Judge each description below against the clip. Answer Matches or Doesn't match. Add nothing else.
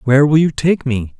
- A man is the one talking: Matches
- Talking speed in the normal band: Doesn't match